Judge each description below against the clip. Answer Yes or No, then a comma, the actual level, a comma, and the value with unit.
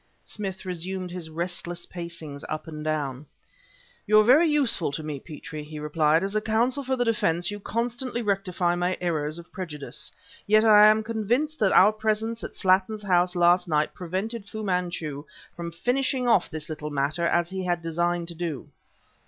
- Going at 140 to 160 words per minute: No, average, 175 wpm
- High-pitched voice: No, medium, 180 Hz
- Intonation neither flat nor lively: Yes, average, 4.8 semitones